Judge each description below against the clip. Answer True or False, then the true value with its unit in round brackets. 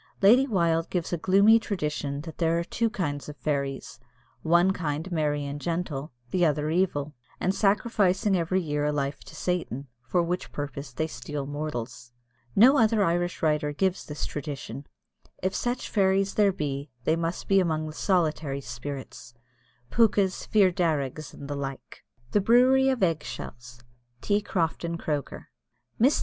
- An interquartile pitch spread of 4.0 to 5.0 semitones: True (4.7 semitones)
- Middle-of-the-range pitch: True (165 Hz)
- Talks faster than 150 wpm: True (160 wpm)